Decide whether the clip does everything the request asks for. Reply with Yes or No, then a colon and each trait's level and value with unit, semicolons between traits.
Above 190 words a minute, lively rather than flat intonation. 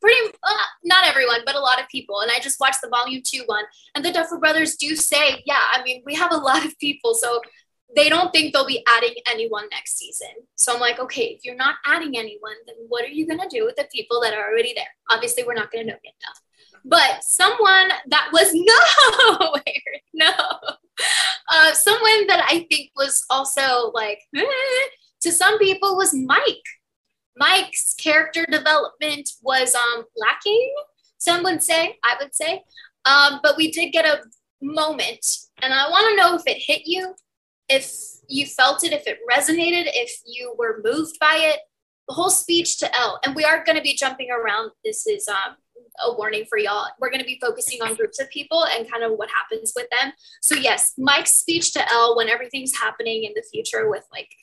Yes: average, 200 wpm; wide, 6.5 semitones